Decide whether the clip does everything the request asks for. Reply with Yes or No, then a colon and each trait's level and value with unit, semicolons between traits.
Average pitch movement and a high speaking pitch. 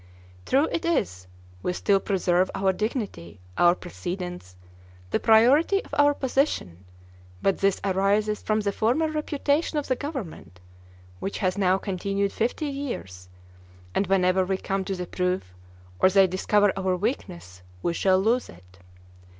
Yes: average, 4.9 semitones; high, 195 Hz